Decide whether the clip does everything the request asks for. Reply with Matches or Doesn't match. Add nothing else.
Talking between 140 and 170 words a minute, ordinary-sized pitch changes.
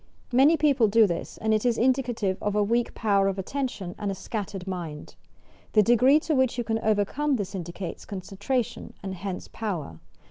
Doesn't match